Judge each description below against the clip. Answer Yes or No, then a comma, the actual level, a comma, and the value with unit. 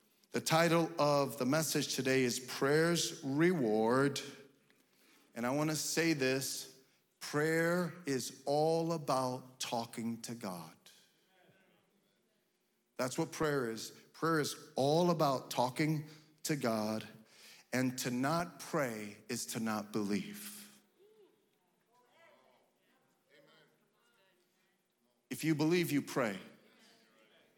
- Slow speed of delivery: Yes, slow, 100 wpm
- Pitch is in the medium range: Yes, medium, 145 Hz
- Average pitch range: Yes, average, 4.7 semitones